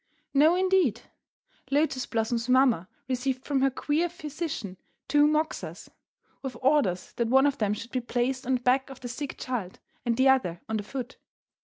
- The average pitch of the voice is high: Yes, very high, 260 Hz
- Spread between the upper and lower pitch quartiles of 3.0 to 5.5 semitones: Yes, average, 3.4 semitones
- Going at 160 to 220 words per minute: Yes, average, 180 wpm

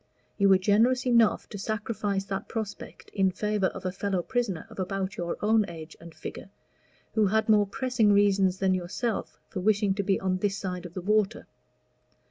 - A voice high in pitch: Yes, high, 200 Hz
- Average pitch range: No, narrow, 2.2 semitones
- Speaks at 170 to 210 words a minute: Yes, average, 185 wpm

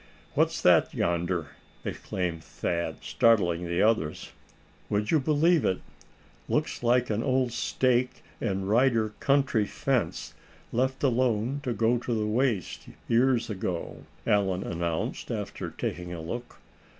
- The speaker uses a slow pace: Yes, slow, 125 wpm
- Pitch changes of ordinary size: No, wide, 5.7 semitones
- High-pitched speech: No, low, 115 Hz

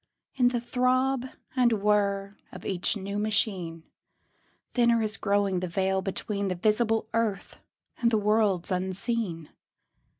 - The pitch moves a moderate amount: Yes, average, 3.3 semitones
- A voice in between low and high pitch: No, high, 210 Hz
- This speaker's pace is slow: Yes, slow, 130 wpm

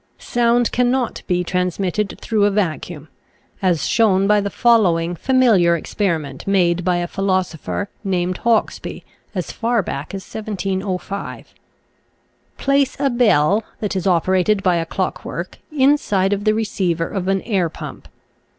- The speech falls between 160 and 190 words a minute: No, average, 140 wpm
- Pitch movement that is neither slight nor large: Yes, average, 3.7 semitones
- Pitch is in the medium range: No, high, 195 Hz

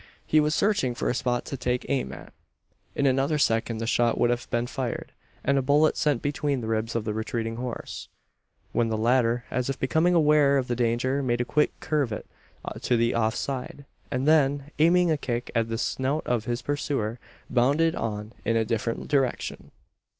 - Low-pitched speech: Yes, low, 125 Hz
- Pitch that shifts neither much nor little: Yes, average, 3.5 semitones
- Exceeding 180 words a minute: Yes, average, 195 wpm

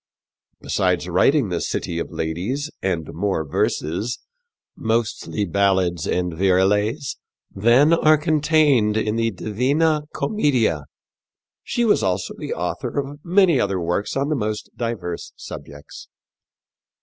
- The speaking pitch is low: Yes, low, 110 Hz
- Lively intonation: Yes, wide, 7.9 semitones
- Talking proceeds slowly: Yes, slow, 120 wpm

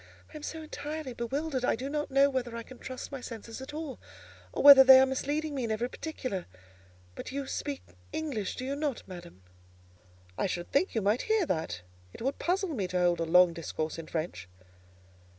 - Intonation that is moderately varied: No, wide, 7.0 semitones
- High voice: Yes, very high, 260 Hz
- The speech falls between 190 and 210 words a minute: Yes, fast, 205 wpm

